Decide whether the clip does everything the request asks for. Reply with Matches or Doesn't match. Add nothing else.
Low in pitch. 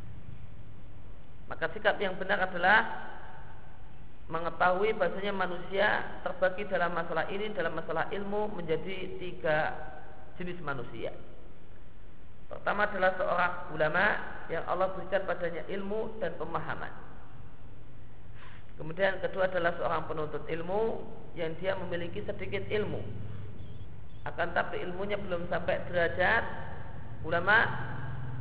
Doesn't match